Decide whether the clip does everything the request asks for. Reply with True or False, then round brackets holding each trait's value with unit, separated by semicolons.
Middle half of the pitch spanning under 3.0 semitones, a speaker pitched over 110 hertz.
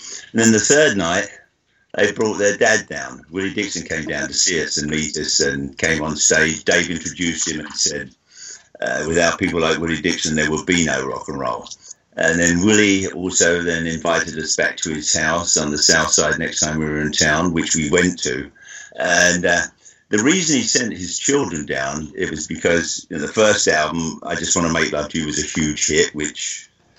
False (2.6 semitones; 80 Hz)